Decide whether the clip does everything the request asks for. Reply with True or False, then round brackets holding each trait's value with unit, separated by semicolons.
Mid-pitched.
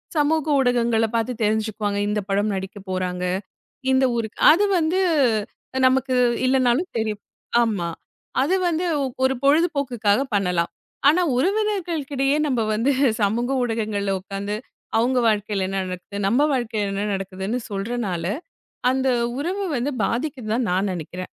False (230 Hz)